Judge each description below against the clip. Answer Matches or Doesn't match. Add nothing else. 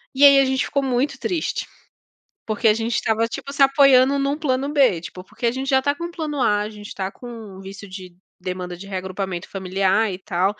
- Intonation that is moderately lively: Doesn't match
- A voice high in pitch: Matches